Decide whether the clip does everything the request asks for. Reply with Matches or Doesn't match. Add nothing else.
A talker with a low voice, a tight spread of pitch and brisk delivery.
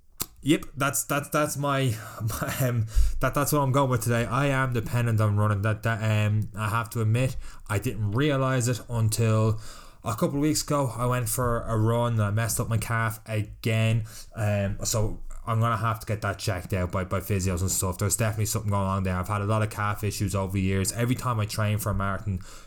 Doesn't match